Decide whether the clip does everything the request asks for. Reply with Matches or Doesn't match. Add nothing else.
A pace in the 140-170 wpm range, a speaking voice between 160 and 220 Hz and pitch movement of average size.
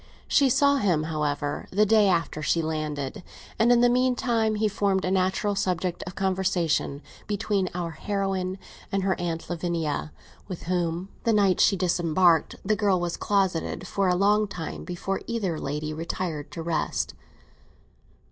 Matches